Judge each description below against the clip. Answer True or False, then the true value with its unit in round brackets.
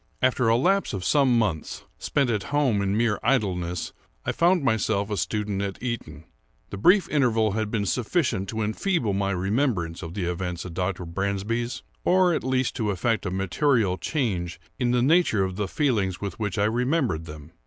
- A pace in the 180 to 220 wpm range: True (185 wpm)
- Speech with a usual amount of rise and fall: True (5.0 semitones)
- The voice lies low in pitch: True (105 Hz)